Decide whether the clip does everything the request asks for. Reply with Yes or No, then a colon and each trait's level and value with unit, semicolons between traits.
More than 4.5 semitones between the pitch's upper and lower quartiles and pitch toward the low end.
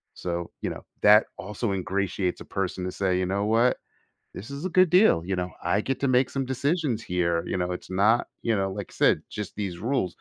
Yes: wide, 5.4 semitones; low, 100 Hz